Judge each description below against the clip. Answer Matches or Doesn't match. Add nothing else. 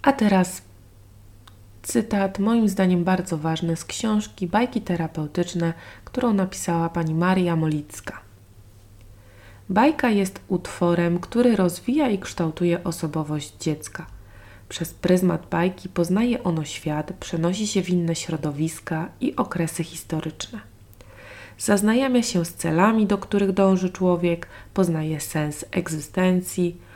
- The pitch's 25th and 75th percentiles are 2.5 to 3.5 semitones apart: Doesn't match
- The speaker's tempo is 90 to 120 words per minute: Matches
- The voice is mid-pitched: Matches